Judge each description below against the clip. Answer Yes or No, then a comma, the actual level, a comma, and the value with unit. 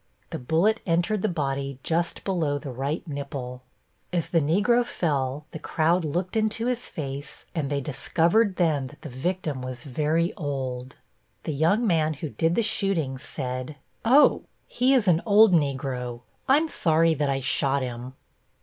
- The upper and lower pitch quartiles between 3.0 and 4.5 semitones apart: No, average, 4.9 semitones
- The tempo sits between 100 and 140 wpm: No, average, 160 wpm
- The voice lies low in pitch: No, medium, 155 Hz